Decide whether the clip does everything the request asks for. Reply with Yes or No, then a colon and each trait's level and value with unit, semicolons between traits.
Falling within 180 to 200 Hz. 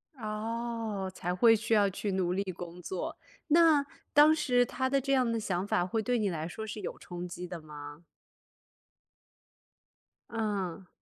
No: high, 210 Hz